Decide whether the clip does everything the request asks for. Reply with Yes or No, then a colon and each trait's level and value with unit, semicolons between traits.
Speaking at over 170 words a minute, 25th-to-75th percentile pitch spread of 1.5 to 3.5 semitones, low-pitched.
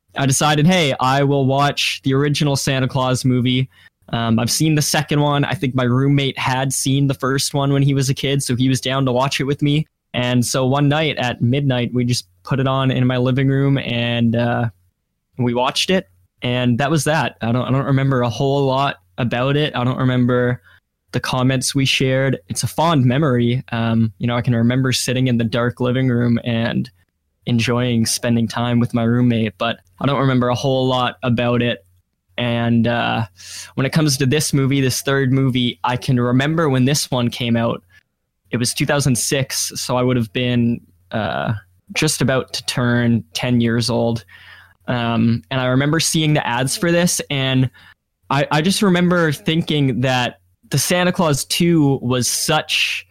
Yes: average, 190 wpm; average, 2.7 semitones; low, 125 Hz